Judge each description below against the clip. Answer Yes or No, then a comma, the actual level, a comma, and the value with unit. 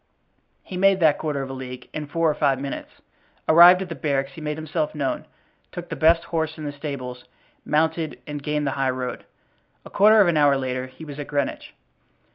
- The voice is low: No, medium, 150 Hz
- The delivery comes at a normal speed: No, fast, 210 wpm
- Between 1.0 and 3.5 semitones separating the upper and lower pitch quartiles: Yes, average, 2.9 semitones